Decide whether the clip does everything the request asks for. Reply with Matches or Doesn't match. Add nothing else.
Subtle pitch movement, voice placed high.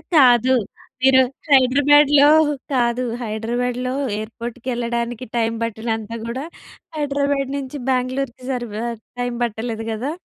Matches